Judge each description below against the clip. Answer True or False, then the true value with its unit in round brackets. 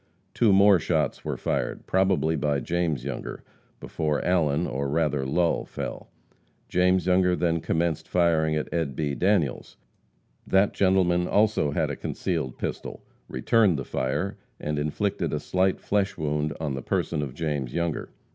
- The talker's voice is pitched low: True (80 Hz)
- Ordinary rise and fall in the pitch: True (3.8 semitones)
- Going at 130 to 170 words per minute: True (150 wpm)